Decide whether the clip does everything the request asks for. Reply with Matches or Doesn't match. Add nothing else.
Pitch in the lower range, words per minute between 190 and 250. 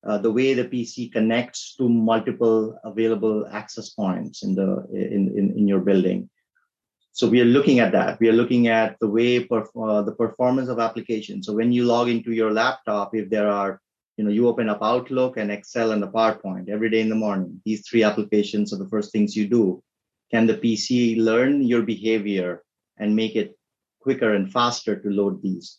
Matches